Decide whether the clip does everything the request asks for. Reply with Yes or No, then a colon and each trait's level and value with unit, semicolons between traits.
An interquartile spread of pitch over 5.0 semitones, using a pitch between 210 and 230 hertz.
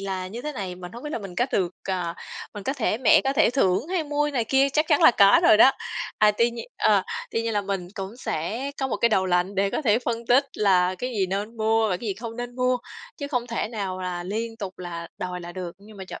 No: average, 4.5 semitones; high, 215 Hz